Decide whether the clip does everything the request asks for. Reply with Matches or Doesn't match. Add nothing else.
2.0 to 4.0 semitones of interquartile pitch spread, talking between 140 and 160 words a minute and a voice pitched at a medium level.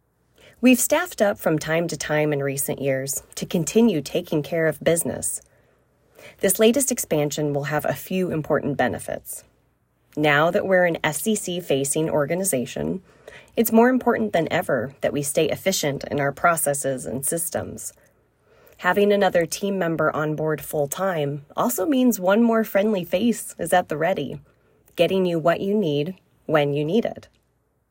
Doesn't match